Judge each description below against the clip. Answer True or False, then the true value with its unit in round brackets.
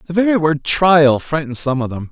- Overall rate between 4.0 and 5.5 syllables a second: True (5.1 syllables/s)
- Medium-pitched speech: True (155 Hz)